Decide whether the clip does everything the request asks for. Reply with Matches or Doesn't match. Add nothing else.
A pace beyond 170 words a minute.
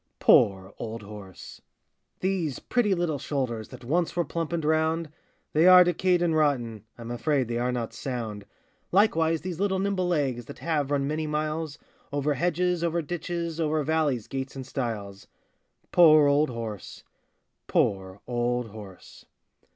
Doesn't match